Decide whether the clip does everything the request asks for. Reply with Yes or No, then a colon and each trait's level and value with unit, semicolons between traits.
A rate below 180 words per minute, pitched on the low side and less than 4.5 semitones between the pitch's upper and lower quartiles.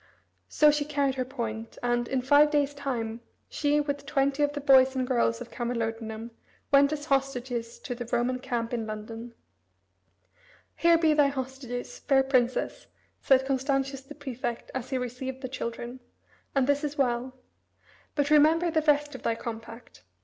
No: average, 165 wpm; very high, 265 Hz; average, 3.0 semitones